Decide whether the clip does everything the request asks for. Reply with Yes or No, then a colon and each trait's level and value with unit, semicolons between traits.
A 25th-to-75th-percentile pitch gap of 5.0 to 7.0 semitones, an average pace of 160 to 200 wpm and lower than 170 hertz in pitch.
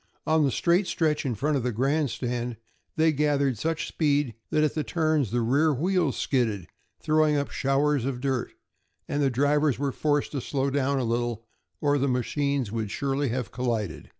No: average, 3.3 semitones; average, 180 wpm; medium, 140 Hz